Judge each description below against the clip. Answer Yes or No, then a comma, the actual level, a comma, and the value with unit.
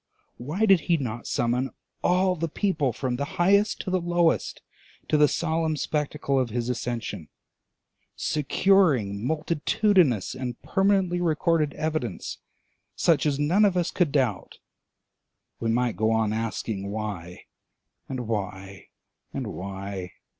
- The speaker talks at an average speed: No, slow, 130 wpm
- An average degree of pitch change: No, wide, 7.4 semitones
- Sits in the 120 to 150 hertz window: Yes, medium, 140 Hz